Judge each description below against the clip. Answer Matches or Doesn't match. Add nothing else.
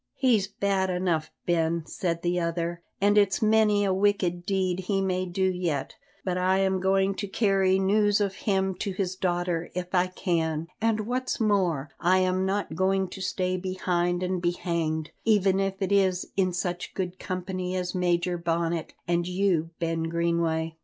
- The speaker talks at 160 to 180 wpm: Matches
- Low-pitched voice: Doesn't match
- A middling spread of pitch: Doesn't match